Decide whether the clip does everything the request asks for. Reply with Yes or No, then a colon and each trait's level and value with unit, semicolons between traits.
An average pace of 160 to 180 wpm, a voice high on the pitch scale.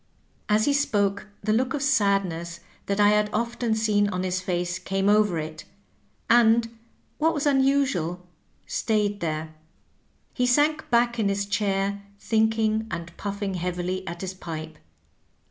No: average, 145 wpm; high, 205 Hz